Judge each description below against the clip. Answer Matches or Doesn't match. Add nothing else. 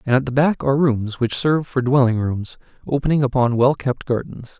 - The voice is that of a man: Matches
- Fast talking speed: Matches